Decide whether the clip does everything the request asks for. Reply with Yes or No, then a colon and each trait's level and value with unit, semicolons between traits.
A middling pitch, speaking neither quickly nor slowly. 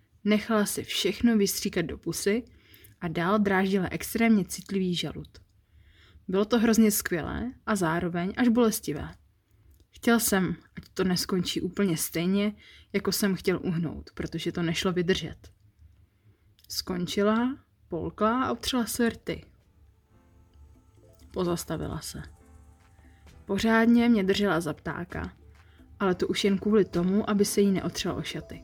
Yes: medium, 175 Hz; average, 125 wpm